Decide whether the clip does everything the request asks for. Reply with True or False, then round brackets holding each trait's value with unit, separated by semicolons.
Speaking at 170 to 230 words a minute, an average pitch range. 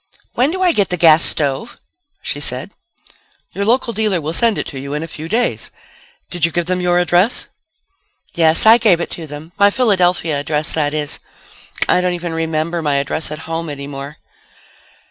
True (190 wpm; 4.0 semitones)